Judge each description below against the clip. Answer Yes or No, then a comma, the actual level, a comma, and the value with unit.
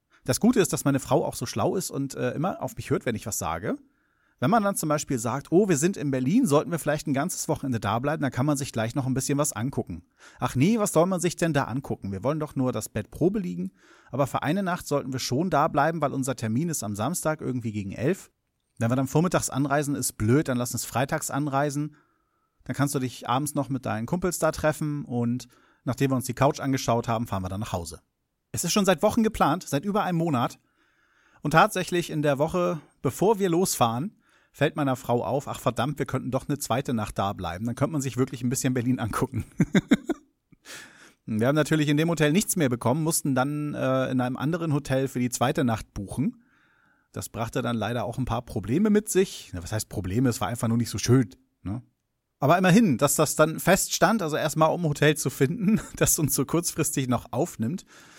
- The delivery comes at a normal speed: No, fast, 230 wpm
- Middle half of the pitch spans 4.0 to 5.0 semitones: Yes, average, 4.6 semitones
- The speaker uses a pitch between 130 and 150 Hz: Yes, medium, 140 Hz